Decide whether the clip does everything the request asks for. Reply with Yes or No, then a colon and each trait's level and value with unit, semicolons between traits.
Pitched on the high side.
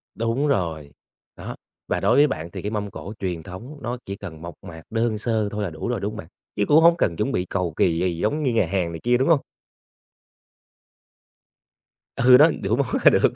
No: low, 105 Hz